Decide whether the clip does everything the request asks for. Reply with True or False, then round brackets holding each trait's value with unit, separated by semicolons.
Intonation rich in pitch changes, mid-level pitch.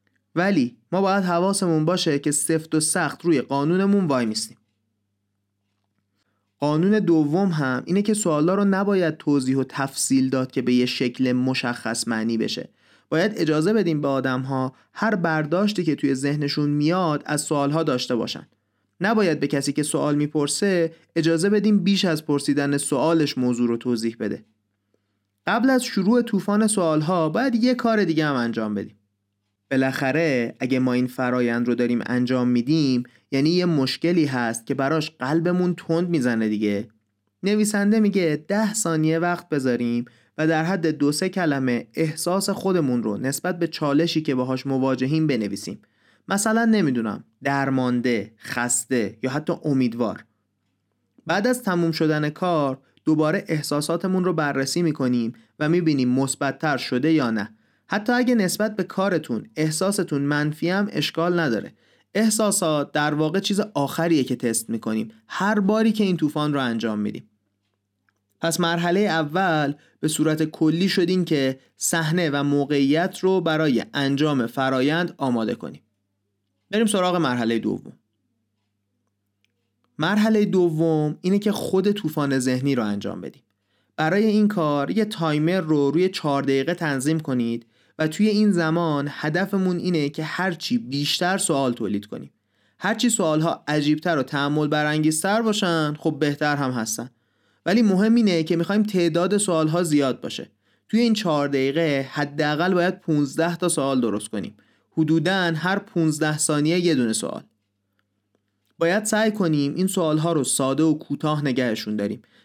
True (6.0 semitones; 150 Hz)